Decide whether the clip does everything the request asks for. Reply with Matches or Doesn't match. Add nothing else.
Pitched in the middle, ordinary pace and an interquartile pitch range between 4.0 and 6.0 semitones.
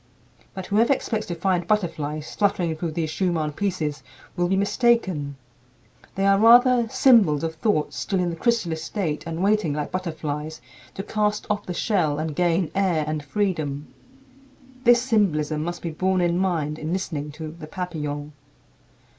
Matches